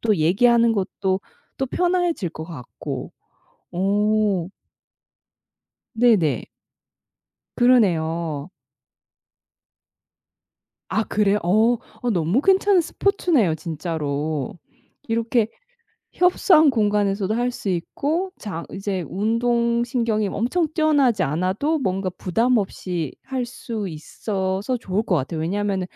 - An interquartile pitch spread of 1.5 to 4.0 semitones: No, average, 5.2 semitones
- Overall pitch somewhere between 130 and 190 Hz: No, high, 210 Hz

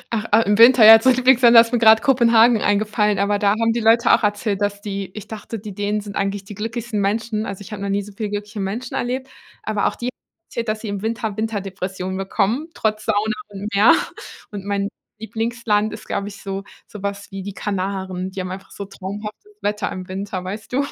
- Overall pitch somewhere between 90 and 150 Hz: No, high, 210 Hz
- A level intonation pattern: Yes, narrow, 2.1 semitones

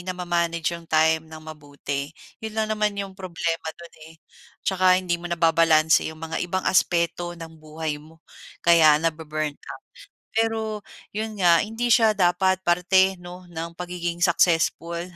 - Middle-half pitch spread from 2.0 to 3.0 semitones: Yes, narrow, 2.5 semitones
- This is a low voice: No, medium, 170 Hz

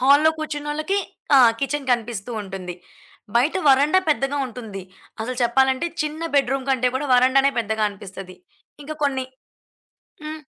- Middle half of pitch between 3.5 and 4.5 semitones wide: Yes, average, 3.8 semitones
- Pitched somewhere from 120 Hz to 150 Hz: No, very high, 265 Hz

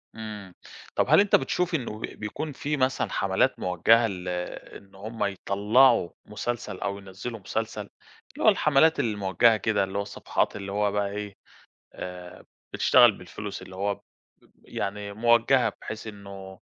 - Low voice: Yes, low, 105 Hz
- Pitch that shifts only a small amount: No, average, 3.1 semitones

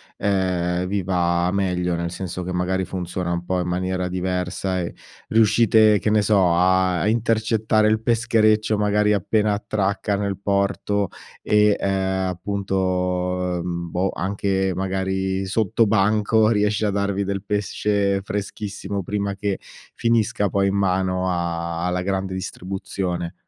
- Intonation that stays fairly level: Yes, narrow, 2.1 semitones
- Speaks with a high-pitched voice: No, very low, 95 Hz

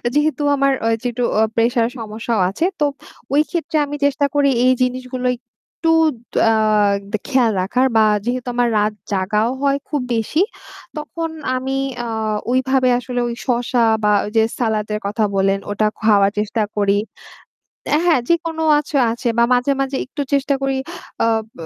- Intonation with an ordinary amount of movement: Yes, average, 4.1 semitones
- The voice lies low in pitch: No, very high, 250 Hz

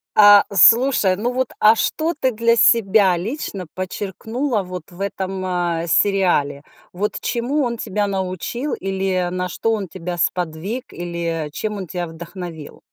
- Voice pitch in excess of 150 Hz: Yes, high, 190 Hz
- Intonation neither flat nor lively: Yes, average, 4.0 semitones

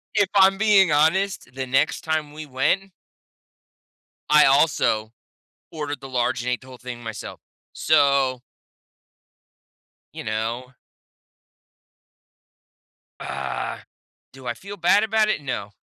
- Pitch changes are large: Yes, wide, 6.7 semitones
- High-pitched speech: No, medium, 145 Hz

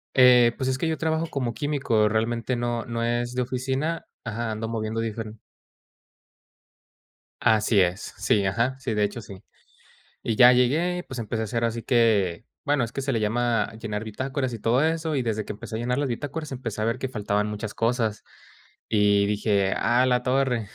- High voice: No, low, 115 Hz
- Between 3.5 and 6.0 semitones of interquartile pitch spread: No, average, 3.1 semitones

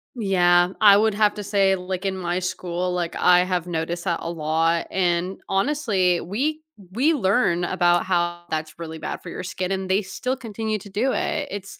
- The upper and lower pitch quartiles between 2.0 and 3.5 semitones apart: Yes, average, 2.8 semitones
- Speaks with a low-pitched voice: No, medium, 185 Hz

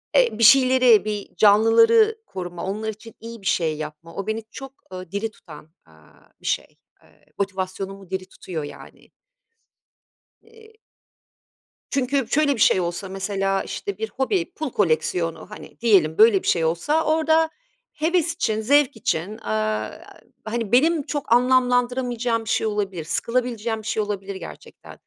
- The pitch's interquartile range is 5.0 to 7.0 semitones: Yes, average, 5.3 semitones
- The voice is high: Yes, high, 215 Hz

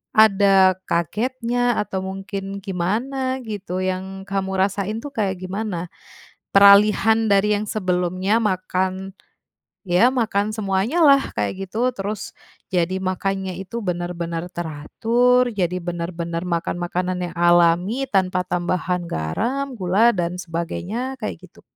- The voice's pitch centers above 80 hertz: Yes, high, 190 Hz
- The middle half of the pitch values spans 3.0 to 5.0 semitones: Yes, average, 3.3 semitones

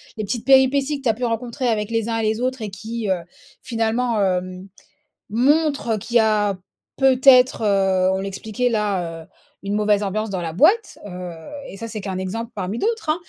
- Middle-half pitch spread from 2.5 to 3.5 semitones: No, average, 4.1 semitones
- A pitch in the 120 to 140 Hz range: No, high, 220 Hz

